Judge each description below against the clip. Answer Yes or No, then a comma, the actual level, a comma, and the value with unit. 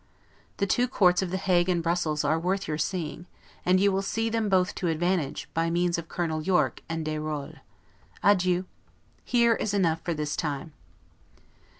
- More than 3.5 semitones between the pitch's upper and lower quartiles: No, average, 3.2 semitones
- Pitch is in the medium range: Yes, medium, 175 Hz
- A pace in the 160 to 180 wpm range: Yes, average, 175 wpm